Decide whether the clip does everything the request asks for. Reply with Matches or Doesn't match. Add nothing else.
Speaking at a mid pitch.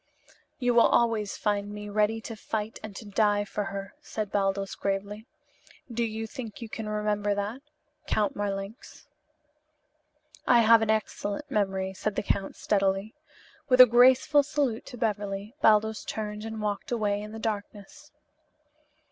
Doesn't match